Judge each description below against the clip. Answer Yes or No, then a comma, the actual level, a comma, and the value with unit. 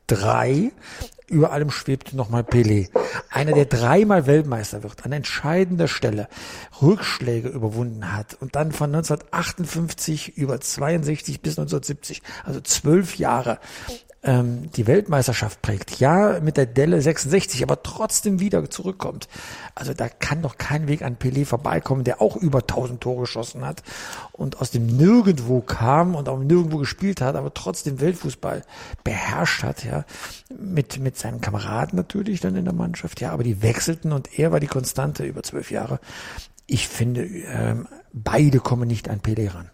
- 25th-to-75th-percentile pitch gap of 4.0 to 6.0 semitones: Yes, average, 5.1 semitones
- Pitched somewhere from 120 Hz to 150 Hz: Yes, low, 135 Hz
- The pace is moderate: Yes, average, 155 wpm